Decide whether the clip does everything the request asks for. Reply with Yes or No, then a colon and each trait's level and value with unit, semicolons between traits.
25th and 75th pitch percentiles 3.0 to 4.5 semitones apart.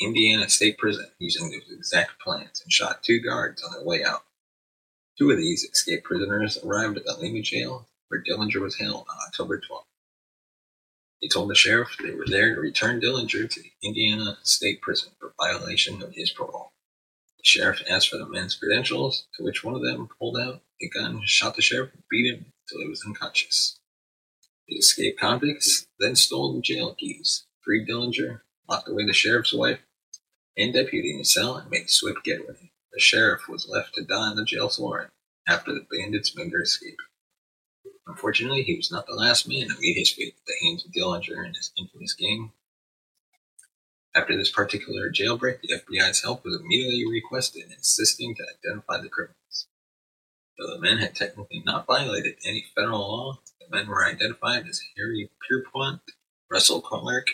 No: average, 5.0 semitones